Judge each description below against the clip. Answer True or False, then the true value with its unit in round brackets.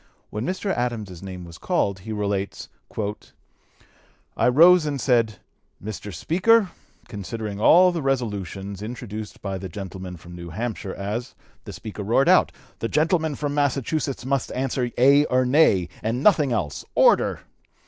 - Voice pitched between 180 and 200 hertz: False (115 Hz)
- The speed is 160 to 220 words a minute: False (145 wpm)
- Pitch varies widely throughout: True (6.1 semitones)